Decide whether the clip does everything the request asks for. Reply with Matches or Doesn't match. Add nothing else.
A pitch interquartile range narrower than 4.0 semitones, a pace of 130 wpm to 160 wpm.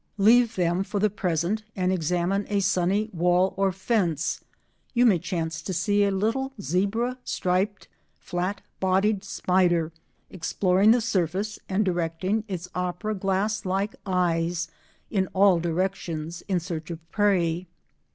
Matches